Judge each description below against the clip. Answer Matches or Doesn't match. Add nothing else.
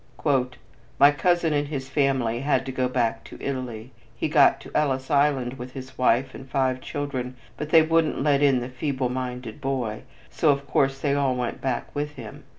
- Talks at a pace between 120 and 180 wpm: Doesn't match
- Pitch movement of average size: Doesn't match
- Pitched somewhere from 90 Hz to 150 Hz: Matches